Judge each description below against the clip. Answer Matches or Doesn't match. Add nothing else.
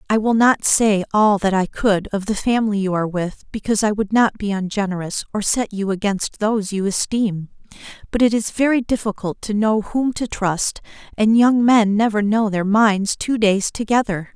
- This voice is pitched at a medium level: Doesn't match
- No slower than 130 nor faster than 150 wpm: Doesn't match